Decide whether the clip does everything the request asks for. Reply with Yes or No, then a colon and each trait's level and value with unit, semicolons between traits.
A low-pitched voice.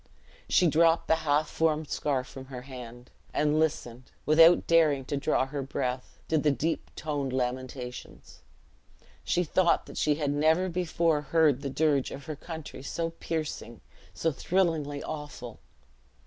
No: medium, 150 Hz